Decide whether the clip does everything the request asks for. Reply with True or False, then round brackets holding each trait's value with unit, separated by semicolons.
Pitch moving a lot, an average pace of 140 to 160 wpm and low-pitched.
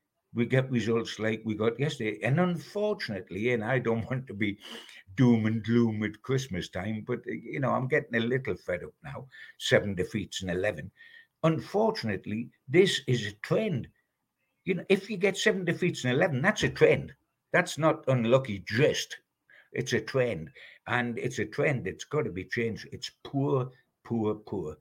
False (5.9 semitones; 175 wpm; 125 Hz)